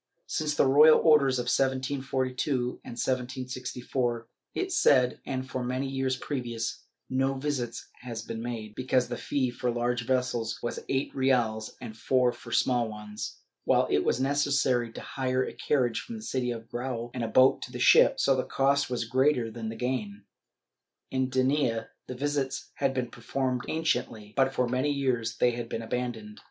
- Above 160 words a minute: Yes, average, 175 wpm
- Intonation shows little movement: Yes, narrow, 2.1 semitones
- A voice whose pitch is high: No, low, 130 Hz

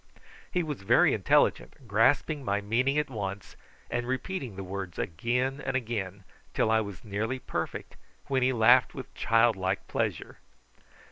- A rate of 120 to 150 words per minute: Yes, average, 145 wpm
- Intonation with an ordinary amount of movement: Yes, average, 4.5 semitones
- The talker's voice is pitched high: No, low, 115 Hz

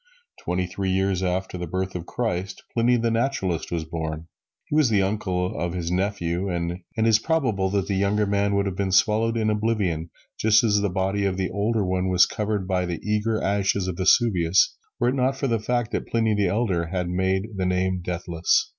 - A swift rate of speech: Yes, fast, 210 wpm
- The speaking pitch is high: No, very low, 95 Hz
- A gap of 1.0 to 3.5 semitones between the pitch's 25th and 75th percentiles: Yes, average, 3.0 semitones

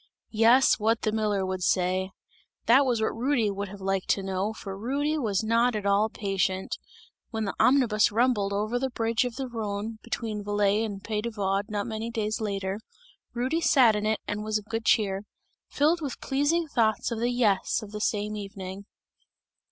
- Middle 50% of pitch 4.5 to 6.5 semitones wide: No, average, 2.8 semitones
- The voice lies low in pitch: No, high, 215 Hz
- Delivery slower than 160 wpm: No, average, 190 wpm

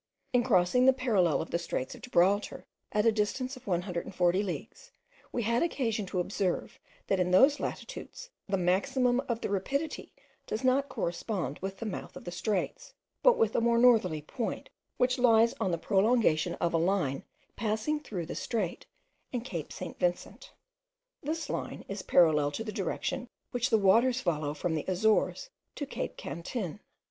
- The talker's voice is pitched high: Yes, high, 210 Hz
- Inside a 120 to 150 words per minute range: No, average, 170 wpm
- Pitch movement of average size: No, wide, 5.7 semitones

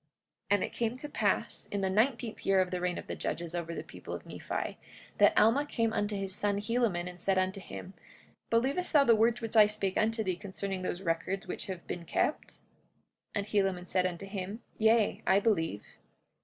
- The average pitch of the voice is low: No, high, 200 Hz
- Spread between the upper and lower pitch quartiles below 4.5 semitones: Yes, average, 3.4 semitones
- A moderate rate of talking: No, fast, 210 wpm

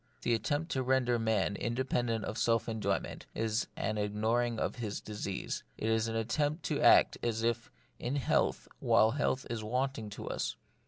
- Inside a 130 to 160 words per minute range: No, average, 170 wpm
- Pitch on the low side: Yes, low, 115 Hz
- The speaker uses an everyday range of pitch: No, narrow, 2.1 semitones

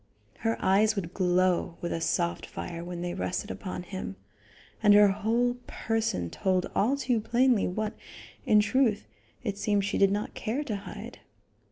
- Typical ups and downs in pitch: Yes, average, 3.6 semitones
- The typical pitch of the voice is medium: No, high, 205 Hz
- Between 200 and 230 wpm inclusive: No, average, 165 wpm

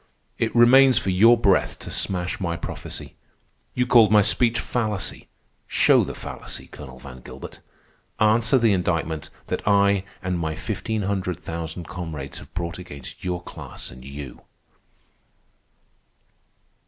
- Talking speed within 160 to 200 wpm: No, slow, 135 wpm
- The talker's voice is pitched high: No, very low, 90 Hz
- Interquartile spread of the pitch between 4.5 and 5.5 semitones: Yes, average, 5.1 semitones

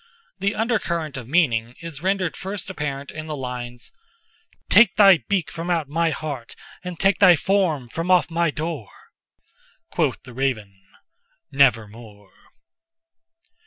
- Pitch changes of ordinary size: No, wide, 6.3 semitones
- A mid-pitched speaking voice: Yes, medium, 160 Hz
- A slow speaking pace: Yes, slow, 125 wpm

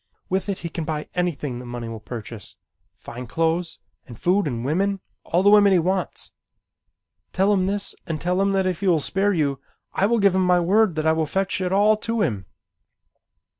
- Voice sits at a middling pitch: Yes, medium, 180 Hz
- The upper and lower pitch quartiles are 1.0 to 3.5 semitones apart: No, average, 4.5 semitones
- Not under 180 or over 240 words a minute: Yes, fast, 205 wpm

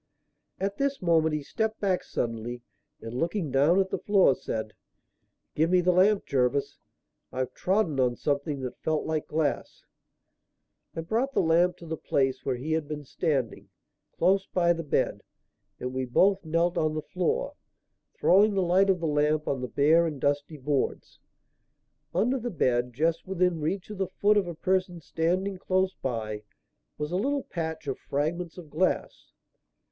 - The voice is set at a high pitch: No, medium, 165 Hz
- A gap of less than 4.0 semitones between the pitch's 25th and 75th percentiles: No, average, 4.8 semitones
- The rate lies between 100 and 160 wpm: No, average, 170 wpm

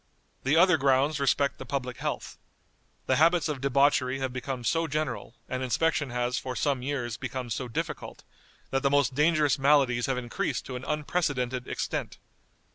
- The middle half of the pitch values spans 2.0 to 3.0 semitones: Yes, narrow, 2.6 semitones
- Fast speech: No, average, 165 wpm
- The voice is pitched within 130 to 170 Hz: Yes, low, 135 Hz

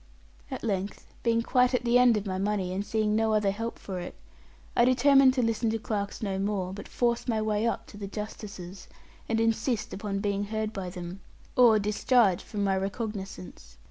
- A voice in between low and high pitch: No, high, 210 Hz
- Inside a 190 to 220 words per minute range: Yes, average, 195 wpm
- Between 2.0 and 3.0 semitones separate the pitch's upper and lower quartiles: Yes, average, 2.7 semitones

